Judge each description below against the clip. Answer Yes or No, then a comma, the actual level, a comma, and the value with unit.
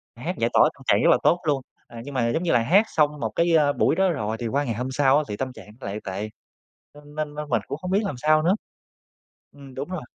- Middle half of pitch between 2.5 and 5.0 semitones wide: Yes, average, 4.0 semitones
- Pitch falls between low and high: Yes, medium, 145 Hz